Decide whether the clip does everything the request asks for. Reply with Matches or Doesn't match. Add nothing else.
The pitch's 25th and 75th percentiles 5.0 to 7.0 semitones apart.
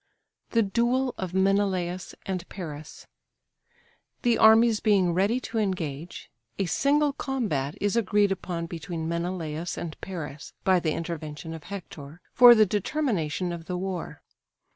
Doesn't match